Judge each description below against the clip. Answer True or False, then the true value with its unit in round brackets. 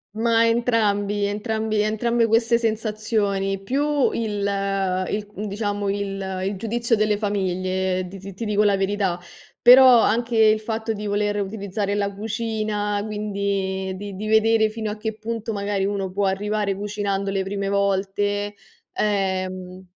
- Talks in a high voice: True (205 Hz)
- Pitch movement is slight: True (1.8 semitones)